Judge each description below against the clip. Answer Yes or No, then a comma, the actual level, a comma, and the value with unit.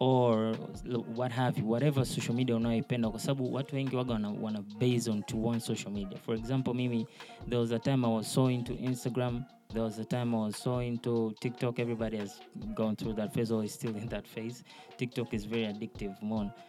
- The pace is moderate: No, fast, 225 wpm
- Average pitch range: No, narrow, 2.0 semitones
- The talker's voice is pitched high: No, low, 115 Hz